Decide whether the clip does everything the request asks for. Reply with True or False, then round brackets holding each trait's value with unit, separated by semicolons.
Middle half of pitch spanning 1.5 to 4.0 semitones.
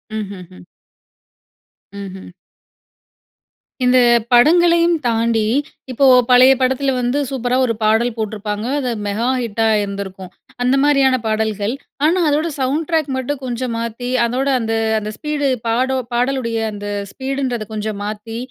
True (3.7 semitones)